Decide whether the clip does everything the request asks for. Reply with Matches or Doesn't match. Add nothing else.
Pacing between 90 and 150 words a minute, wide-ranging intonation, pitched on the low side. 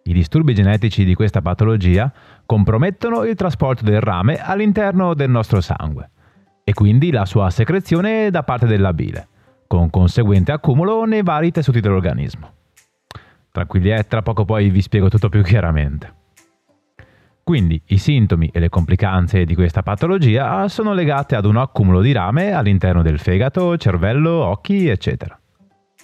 Matches